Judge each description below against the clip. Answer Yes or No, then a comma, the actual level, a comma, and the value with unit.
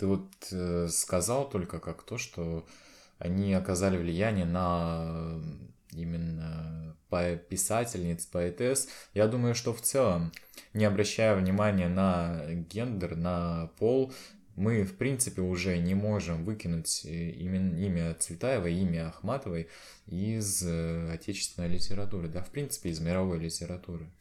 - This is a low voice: Yes, very low, 90 Hz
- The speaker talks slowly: No, average, 120 wpm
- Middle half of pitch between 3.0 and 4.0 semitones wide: Yes, average, 3.5 semitones